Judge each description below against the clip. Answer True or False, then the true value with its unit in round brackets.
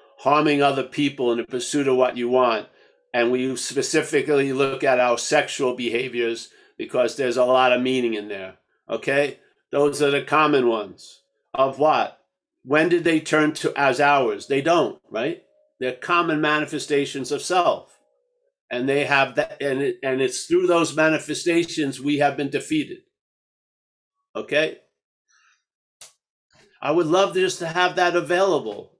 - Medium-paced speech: True (155 wpm)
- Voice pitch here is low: False (145 Hz)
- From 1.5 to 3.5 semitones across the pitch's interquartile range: False (4.5 semitones)